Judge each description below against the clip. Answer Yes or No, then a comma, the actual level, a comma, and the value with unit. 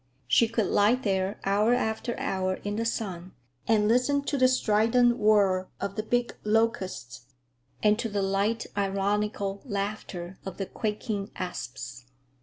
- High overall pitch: Yes, high, 210 Hz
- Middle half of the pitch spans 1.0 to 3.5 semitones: Yes, average, 2.8 semitones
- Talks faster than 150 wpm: No, average, 145 wpm